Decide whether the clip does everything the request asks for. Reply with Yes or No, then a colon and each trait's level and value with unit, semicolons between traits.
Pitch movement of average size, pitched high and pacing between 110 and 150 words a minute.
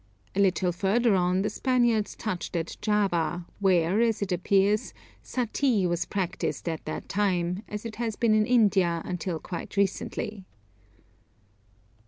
Yes: average, 3.3 semitones; high, 195 Hz; average, 140 wpm